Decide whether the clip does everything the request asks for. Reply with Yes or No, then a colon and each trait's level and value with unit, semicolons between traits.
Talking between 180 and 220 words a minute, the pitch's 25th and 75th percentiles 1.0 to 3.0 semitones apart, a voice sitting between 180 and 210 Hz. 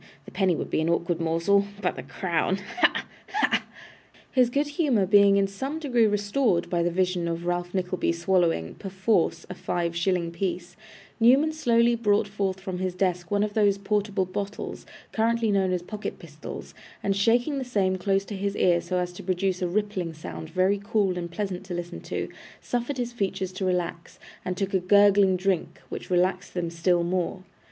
Yes: average, 185 wpm; average, 2.7 semitones; high, 190 Hz